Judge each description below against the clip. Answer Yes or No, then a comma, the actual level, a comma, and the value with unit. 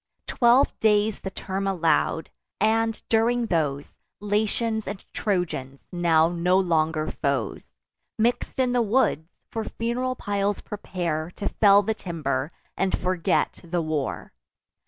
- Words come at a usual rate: No, slow, 125 wpm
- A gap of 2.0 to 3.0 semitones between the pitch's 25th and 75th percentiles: No, average, 5.3 semitones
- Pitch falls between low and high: No, high, 195 Hz